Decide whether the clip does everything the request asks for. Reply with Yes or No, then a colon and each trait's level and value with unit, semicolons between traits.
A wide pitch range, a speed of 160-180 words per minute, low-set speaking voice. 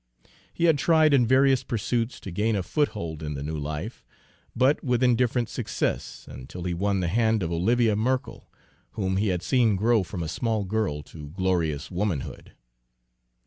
Yes: wide, 5.9 semitones; average, 170 wpm; low, 105 Hz